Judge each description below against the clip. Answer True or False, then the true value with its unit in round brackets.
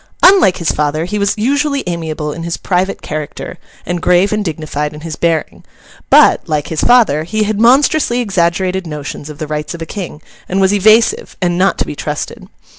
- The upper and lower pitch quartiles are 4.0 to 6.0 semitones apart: True (5.2 semitones)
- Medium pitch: True (175 Hz)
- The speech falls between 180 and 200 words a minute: True (190 wpm)